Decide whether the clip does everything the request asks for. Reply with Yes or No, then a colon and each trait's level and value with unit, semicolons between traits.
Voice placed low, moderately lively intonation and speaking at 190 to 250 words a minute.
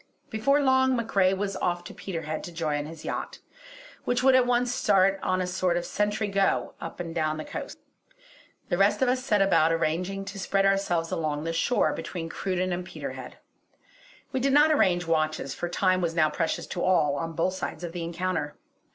No: medium, 185 Hz; average, 3.7 semitones; average, 195 wpm